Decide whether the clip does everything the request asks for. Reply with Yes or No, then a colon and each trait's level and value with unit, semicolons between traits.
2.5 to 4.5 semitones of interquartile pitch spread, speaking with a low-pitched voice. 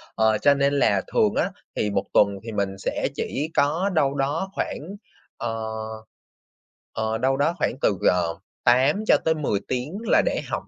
No: average, 5.1 semitones; low, 130 Hz